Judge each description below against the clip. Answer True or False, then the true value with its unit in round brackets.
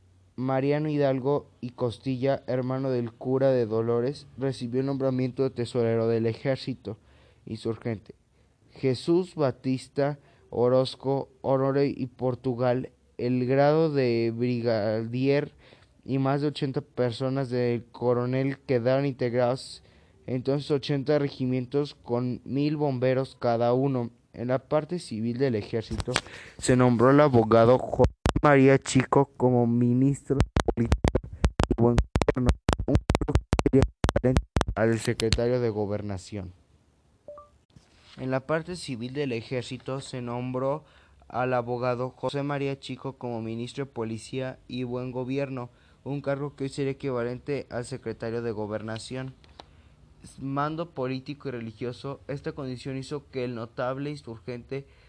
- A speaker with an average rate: False (120 wpm)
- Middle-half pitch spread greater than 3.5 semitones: False (2.5 semitones)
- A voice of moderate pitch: False (130 Hz)